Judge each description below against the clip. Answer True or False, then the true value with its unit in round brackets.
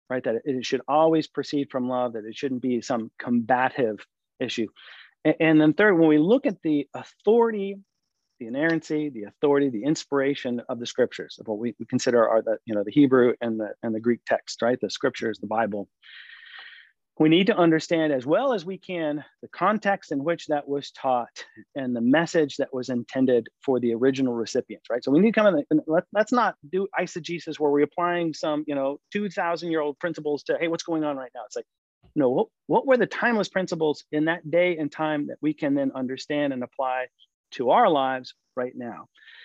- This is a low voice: False (145 Hz)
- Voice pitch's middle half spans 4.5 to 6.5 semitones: True (5.0 semitones)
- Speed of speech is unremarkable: False (210 wpm)